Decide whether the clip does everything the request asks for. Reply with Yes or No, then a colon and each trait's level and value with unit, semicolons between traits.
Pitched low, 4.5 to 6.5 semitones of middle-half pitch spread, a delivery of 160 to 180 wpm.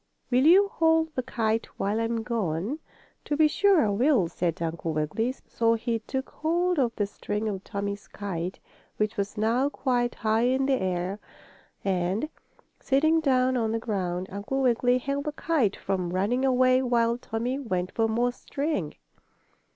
No: high, 230 Hz; average, 4.9 semitones; average, 165 wpm